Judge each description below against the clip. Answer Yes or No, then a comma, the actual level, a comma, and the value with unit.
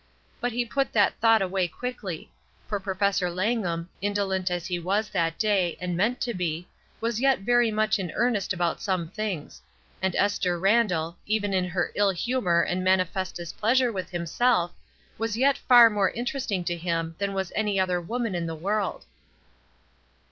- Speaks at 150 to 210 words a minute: Yes, average, 170 wpm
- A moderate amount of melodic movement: Yes, average, 4.0 semitones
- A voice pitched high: Yes, high, 195 Hz